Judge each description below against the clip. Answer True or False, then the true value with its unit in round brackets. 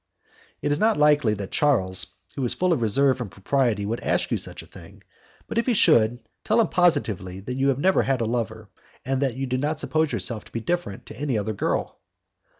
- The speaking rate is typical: False (220 wpm)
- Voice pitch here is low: True (130 Hz)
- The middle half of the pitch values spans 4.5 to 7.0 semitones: True (5.2 semitones)